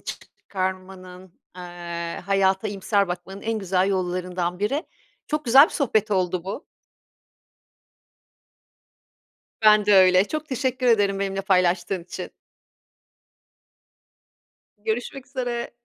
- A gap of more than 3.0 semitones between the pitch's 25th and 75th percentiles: Yes, average, 3.4 semitones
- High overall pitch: Yes, high, 195 Hz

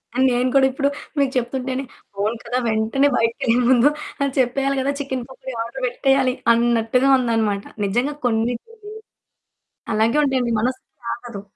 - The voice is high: Yes, very high, 250 Hz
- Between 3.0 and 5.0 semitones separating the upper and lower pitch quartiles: No, narrow, 2.5 semitones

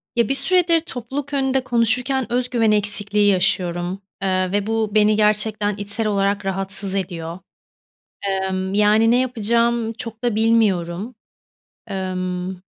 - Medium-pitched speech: No, high, 210 Hz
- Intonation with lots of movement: No, average, 3.5 semitones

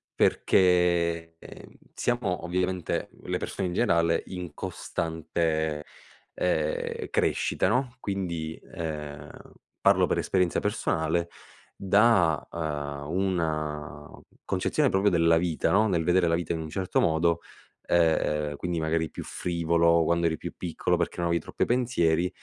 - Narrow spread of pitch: Yes, narrow, 2.3 semitones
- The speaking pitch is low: Yes, very low, 85 Hz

